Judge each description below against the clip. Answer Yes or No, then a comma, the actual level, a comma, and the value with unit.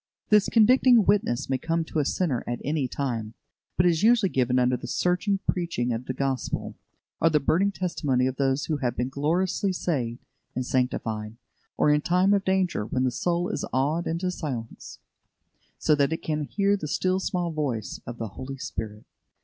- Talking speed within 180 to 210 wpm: Yes, average, 190 wpm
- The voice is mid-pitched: Yes, medium, 150 Hz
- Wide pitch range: Yes, wide, 6.1 semitones